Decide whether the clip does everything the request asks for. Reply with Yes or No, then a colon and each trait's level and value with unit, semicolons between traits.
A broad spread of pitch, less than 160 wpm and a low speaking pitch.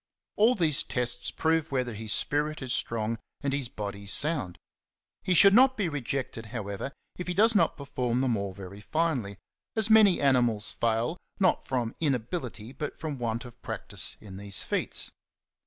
No: wide, 6.4 semitones; average, 165 wpm; low, 130 Hz